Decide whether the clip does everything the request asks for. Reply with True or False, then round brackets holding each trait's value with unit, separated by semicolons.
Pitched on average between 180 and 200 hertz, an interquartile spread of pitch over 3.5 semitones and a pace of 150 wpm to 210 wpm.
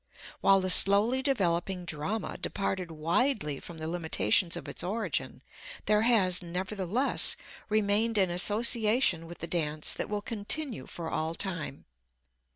False (190 Hz; 4.3 semitones; 135 wpm)